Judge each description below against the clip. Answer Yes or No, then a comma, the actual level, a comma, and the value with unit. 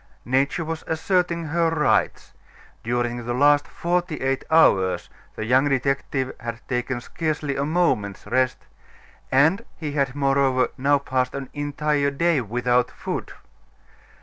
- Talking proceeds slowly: Yes, slow, 130 wpm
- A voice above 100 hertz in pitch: Yes, medium, 140 Hz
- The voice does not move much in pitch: No, average, 3.5 semitones